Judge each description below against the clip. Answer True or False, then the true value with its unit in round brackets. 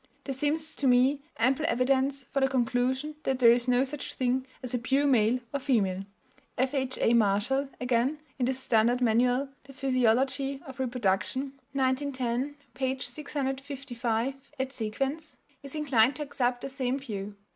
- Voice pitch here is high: True (260 Hz)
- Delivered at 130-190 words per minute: True (150 wpm)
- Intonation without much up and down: True (2.1 semitones)